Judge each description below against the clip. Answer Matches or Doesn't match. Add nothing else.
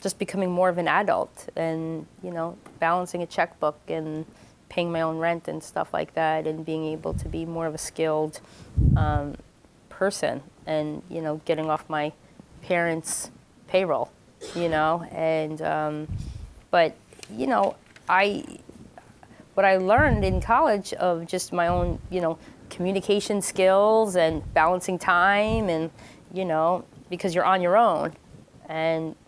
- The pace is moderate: Matches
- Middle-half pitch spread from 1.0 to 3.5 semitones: Matches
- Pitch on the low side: Doesn't match